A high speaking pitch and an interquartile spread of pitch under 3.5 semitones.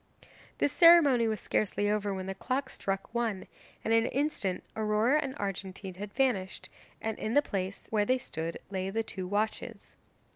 No: high, 210 Hz; average, 4.1 semitones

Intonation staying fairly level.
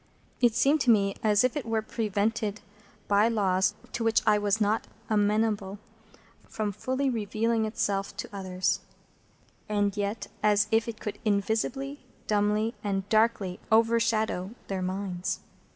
Yes: narrow, 2.1 semitones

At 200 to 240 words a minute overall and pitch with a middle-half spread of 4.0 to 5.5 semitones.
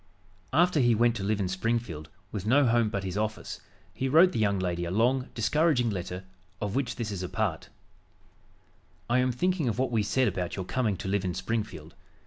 Yes: fast, 205 wpm; average, 4.6 semitones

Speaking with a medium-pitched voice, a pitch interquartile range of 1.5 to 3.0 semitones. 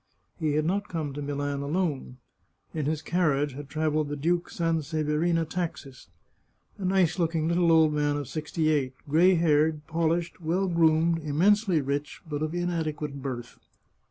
Yes: medium, 155 Hz; narrow, 2.6 semitones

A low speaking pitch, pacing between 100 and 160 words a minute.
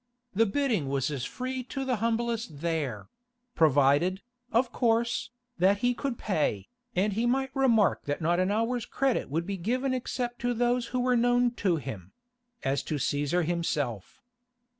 No: high, 225 Hz; average, 155 wpm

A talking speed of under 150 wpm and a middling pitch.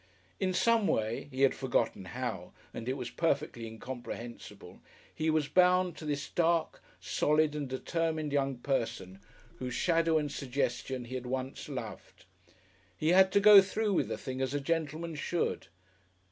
No: average, 160 wpm; medium, 145 Hz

